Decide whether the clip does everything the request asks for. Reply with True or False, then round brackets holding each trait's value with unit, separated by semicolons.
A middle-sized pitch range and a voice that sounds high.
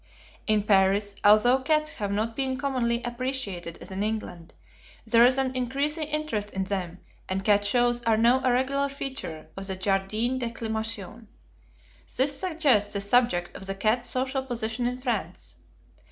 True (4.3 semitones; 230 Hz)